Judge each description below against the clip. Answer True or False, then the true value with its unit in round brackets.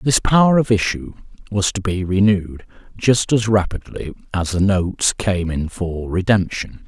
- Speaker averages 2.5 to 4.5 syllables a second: True (4.4 syllables/s)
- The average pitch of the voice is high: False (95 Hz)